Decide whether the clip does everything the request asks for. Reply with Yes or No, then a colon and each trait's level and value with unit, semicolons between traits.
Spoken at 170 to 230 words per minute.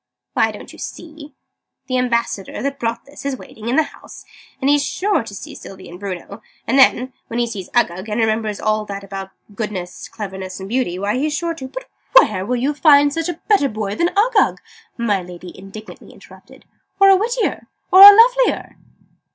Yes: average, 190 wpm